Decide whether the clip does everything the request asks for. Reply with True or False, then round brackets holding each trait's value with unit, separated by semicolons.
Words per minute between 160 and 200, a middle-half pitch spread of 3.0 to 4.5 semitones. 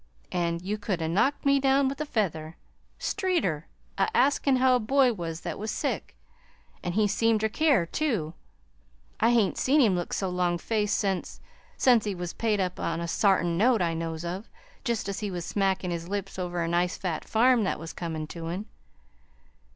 False (190 wpm; 5.1 semitones)